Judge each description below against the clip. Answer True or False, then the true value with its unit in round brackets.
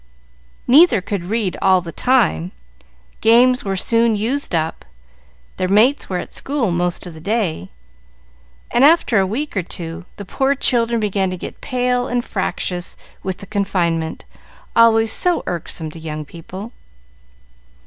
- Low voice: False (200 Hz)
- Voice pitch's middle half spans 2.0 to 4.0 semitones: False (5.3 semitones)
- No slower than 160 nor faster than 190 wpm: False (150 wpm)